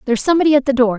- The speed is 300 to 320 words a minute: Yes, fast, 305 wpm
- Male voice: No, female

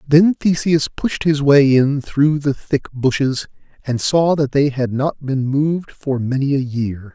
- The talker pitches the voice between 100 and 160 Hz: Yes, medium, 140 Hz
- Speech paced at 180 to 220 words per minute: Yes, average, 185 wpm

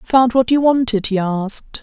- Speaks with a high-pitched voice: Yes, high, 235 Hz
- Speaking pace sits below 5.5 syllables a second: Yes, 4.6 syllables/s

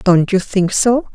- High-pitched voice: Yes, high, 200 Hz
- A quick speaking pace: Yes, fast, 210 wpm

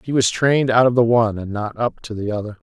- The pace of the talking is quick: Yes, fast, 290 wpm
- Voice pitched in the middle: No, low, 115 Hz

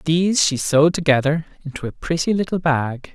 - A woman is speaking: No, male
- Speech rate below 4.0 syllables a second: No, 5.5 syllables/s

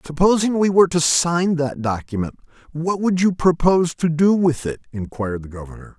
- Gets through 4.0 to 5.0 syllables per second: No, 5.4 syllables/s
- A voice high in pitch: No, medium, 155 Hz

